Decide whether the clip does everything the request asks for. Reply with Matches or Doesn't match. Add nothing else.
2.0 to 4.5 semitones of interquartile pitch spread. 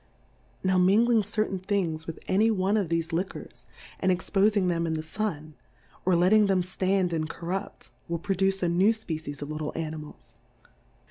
Matches